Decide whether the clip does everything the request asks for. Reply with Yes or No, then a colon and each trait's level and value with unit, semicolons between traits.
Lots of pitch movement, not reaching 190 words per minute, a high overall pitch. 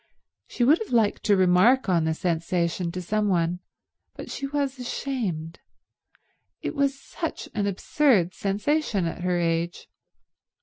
Yes: wide, 7.0 semitones; average, 140 wpm; high, 195 Hz